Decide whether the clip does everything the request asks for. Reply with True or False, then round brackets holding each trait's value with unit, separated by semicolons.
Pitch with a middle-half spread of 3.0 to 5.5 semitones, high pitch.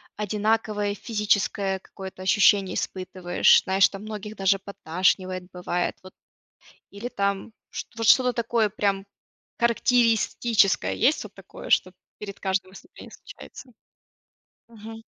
False (2.6 semitones; 200 Hz)